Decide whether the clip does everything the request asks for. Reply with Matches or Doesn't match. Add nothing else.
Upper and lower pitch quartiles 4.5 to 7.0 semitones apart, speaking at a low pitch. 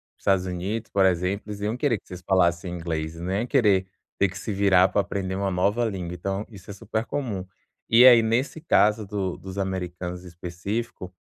Doesn't match